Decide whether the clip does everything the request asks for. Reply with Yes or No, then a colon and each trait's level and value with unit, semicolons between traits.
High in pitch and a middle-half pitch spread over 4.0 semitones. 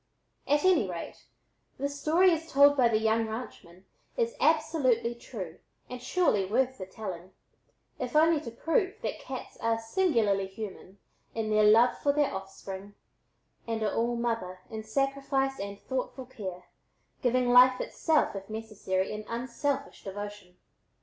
Yes: high, 230 Hz; average, 5.2 semitones